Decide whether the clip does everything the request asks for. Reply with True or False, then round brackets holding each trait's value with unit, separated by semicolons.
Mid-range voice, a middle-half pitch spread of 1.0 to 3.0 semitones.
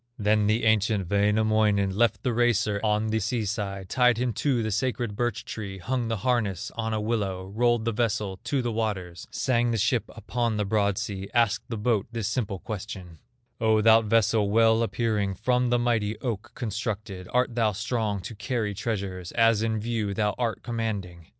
False (110 Hz; 2.4 semitones)